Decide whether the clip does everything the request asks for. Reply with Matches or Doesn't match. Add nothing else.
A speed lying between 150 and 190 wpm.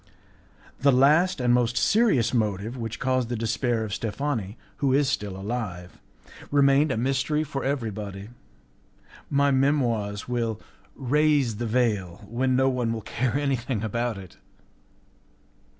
Doesn't match